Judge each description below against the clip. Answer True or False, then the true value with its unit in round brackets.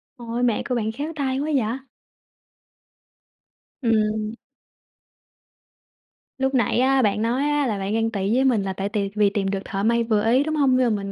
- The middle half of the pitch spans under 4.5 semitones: True (3.9 semitones)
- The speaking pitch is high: True (230 Hz)